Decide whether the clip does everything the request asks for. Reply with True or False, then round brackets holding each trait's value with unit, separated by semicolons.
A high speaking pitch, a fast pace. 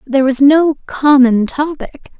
False (275 Hz; 135 wpm)